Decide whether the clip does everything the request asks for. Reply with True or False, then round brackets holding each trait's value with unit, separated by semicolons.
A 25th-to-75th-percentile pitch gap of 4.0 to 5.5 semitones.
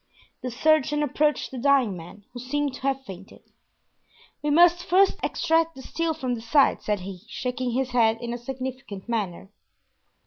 True (4.4 semitones)